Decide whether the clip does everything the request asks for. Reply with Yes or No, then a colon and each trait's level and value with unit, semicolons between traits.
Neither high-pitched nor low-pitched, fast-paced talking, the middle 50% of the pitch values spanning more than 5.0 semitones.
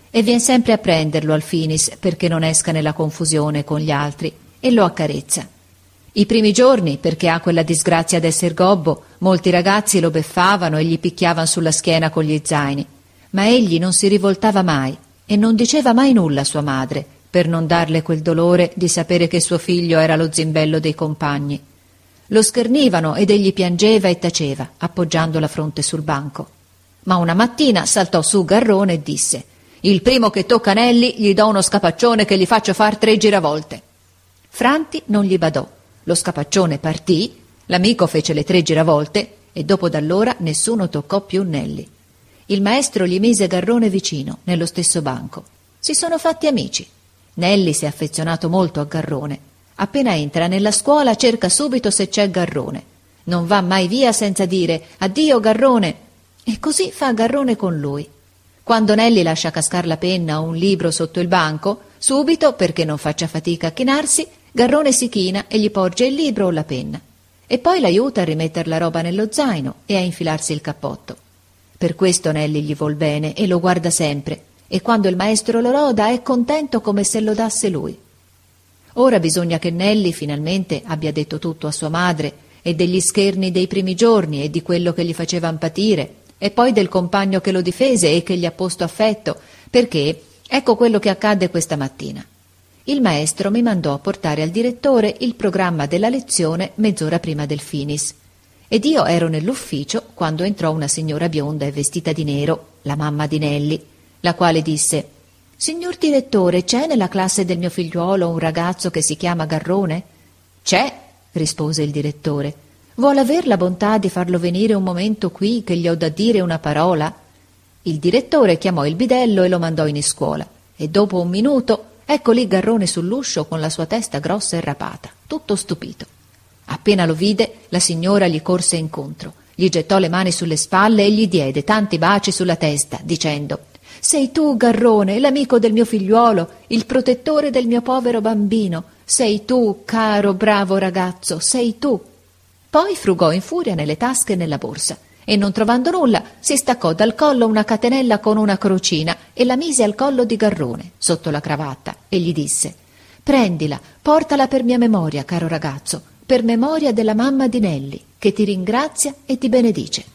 Yes: medium, 180 Hz; fast, 175 wpm; wide, 5.6 semitones